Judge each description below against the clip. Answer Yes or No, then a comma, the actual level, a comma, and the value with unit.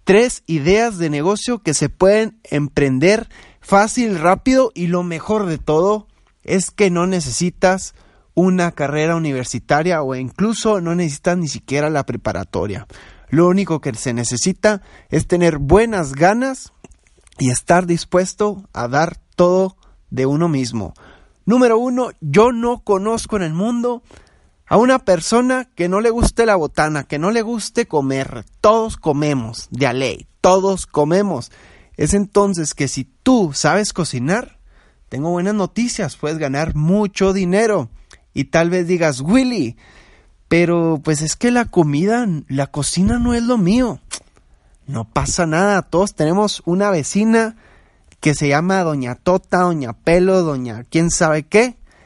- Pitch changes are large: Yes, wide, 6.0 semitones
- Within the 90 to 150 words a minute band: Yes, average, 145 wpm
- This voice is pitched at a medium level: Yes, medium, 175 Hz